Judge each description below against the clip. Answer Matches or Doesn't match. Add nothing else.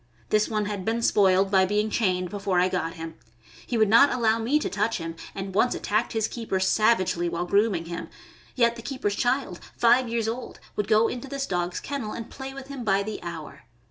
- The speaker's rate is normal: Doesn't match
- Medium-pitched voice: Doesn't match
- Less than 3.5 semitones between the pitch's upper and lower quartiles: Doesn't match